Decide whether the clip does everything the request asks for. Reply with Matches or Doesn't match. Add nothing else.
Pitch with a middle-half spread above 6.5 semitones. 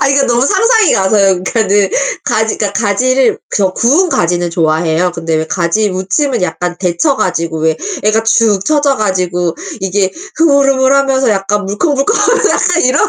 Matches